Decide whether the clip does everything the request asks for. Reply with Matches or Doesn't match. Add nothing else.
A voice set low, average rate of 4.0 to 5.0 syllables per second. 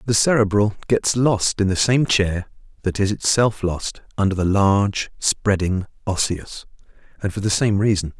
Matches